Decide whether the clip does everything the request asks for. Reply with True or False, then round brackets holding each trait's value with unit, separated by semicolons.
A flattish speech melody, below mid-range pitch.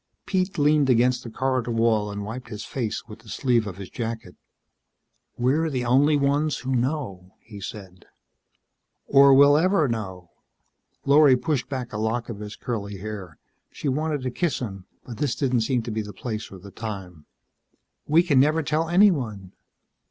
False (5.1 semitones; 120 Hz)